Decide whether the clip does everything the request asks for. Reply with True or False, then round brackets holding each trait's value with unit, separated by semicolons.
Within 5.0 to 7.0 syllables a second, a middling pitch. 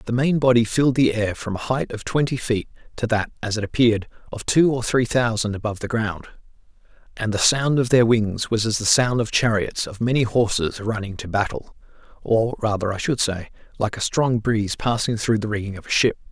False (5.5 syllables/s; 115 Hz)